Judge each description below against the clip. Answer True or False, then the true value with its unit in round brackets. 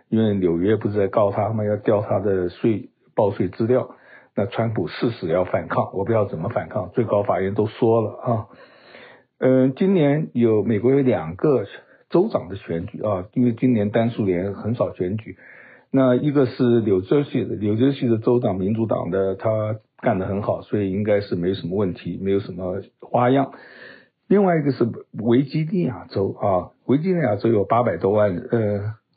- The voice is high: False (115 Hz)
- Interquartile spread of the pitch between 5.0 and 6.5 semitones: False (4.1 semitones)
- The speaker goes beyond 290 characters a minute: False (275 characters per minute)